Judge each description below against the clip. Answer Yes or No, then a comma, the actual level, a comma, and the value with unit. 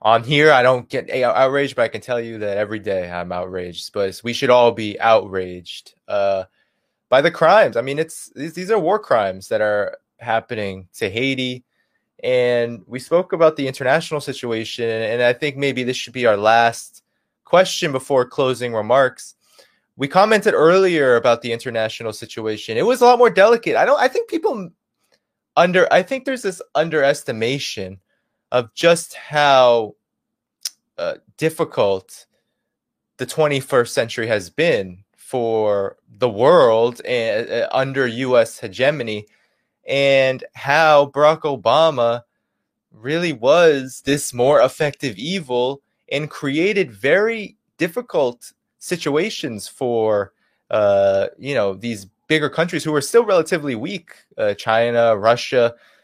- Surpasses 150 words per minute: No, average, 140 wpm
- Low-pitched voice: Yes, low, 130 Hz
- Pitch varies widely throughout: Yes, wide, 5.8 semitones